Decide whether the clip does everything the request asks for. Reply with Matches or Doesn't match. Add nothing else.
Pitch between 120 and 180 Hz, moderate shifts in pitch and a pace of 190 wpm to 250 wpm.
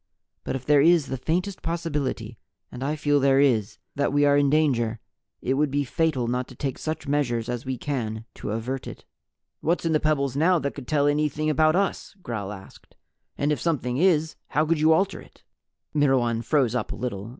Matches